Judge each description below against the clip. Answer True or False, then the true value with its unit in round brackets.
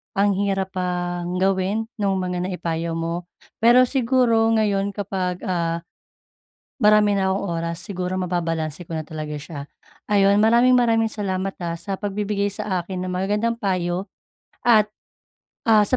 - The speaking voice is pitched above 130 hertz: True (190 Hz)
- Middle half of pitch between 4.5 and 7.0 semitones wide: False (2.9 semitones)